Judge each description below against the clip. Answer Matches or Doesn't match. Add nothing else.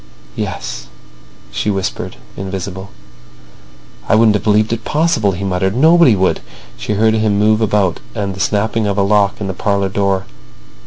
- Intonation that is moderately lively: Doesn't match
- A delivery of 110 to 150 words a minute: Doesn't match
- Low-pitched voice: Matches